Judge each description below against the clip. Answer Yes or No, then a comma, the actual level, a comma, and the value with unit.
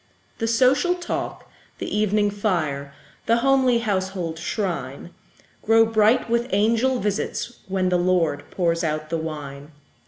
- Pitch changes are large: Yes, wide, 5.7 semitones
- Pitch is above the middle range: Yes, high, 200 Hz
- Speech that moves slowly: Yes, slow, 130 wpm